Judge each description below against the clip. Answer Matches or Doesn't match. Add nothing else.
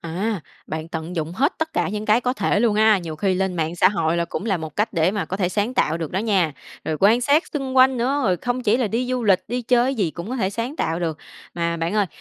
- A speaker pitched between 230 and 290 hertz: Doesn't match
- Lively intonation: Matches